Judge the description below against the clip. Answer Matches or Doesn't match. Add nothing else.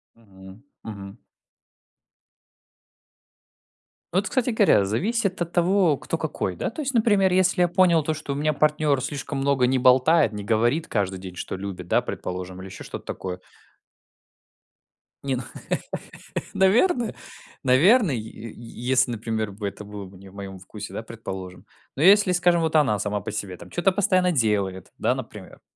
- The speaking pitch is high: Doesn't match